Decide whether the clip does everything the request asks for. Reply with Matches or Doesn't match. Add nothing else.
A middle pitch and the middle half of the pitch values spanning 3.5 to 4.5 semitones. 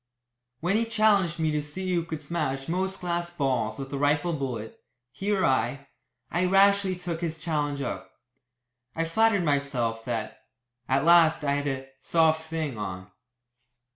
Matches